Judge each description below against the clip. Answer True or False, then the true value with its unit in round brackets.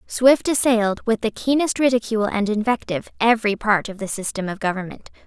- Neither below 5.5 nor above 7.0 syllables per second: True (6.0 syllables/s)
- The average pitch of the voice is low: False (220 Hz)